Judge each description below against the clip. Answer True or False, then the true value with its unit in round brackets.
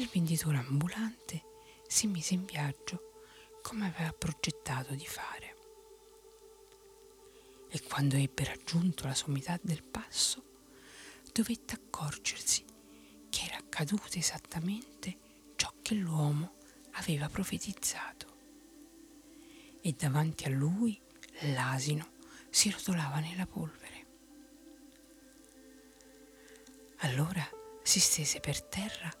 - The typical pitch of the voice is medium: True (180 Hz)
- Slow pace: True (90 wpm)